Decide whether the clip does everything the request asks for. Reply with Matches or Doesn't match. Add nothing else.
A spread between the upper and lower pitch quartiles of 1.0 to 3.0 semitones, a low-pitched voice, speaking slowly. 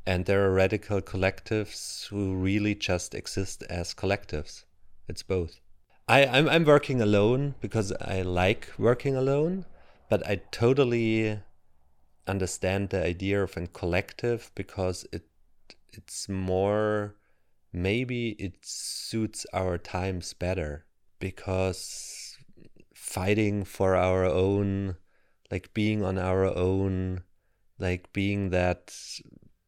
Matches